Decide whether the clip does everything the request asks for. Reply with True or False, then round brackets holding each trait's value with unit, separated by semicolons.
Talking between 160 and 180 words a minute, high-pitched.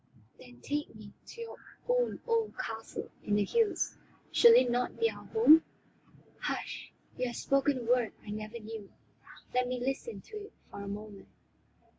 True (170 wpm; 250 Hz)